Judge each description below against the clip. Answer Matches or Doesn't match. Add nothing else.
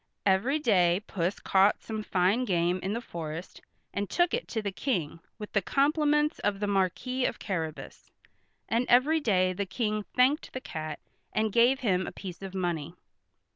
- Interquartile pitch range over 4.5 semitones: Matches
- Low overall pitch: Doesn't match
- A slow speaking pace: Doesn't match